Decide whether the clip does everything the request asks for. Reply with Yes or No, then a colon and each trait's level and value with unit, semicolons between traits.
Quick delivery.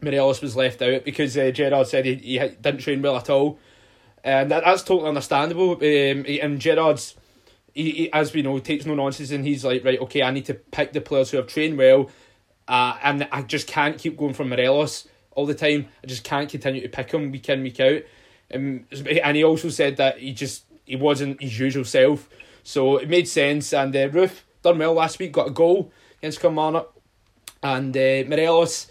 Yes: fast, 210 wpm